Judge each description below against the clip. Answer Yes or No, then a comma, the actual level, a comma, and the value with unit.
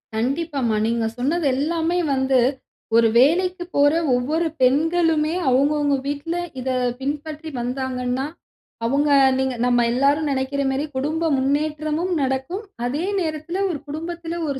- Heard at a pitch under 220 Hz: No, very high, 290 Hz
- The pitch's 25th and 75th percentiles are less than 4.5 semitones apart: Yes, average, 3.5 semitones